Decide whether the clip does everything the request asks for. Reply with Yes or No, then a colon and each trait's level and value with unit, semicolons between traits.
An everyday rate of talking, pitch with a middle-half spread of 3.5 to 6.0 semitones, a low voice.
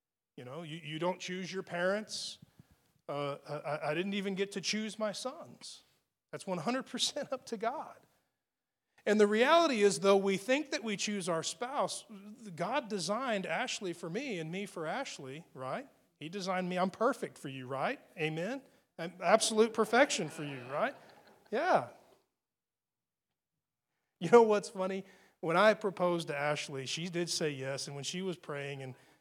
No: average, 165 wpm; average, 5.2 semitones; high, 190 Hz